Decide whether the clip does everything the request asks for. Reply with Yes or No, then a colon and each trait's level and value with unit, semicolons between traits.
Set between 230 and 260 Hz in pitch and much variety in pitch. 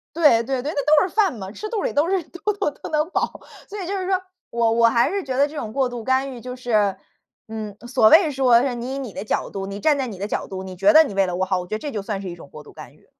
Yes: very high, 250 Hz; wide, 6.3 semitones